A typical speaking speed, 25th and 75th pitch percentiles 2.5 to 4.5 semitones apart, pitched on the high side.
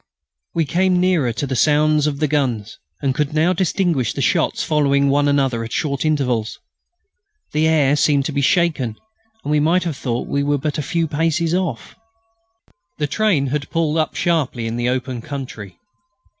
No: average, 180 wpm; average, 3.2 semitones; medium, 145 Hz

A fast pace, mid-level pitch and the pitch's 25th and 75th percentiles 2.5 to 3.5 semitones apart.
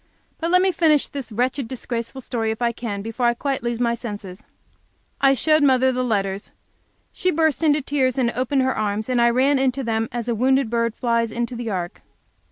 No: fast, 210 wpm; high, 245 Hz; average, 2.9 semitones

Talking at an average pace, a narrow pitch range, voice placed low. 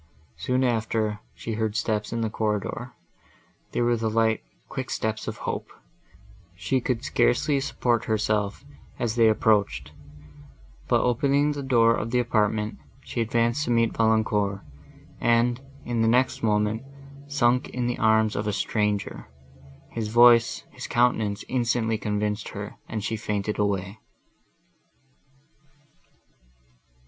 No: slow, 125 wpm; narrow, 2.2 semitones; low, 110 Hz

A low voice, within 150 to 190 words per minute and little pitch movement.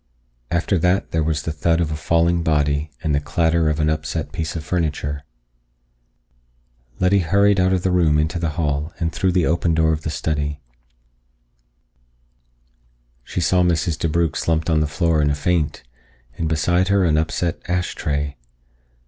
Yes: very low, 80 Hz; average, 170 wpm; narrow, 2.2 semitones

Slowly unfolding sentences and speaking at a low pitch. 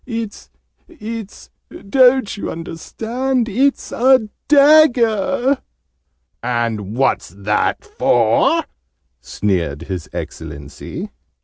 No: slow, 80 wpm; high, 215 Hz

